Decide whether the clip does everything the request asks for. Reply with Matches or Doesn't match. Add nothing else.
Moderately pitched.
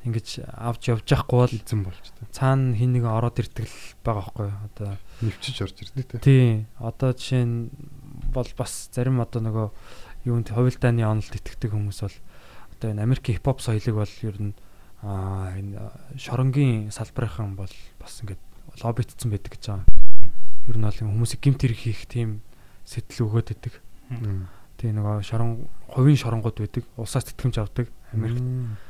Doesn't match